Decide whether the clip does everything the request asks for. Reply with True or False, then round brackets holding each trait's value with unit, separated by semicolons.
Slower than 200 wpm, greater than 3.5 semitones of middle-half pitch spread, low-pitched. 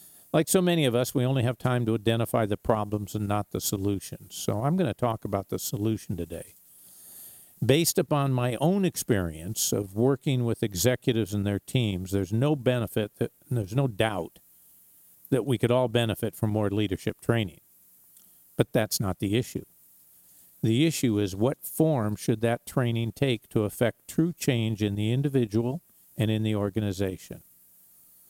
True (170 wpm; 4.1 semitones; 110 Hz)